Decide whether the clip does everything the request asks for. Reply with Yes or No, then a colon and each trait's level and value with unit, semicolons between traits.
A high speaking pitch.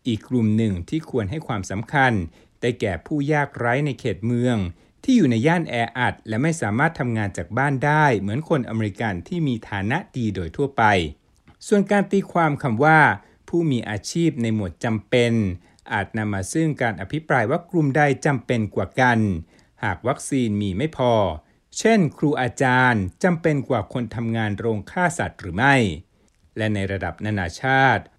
No: low, 120 Hz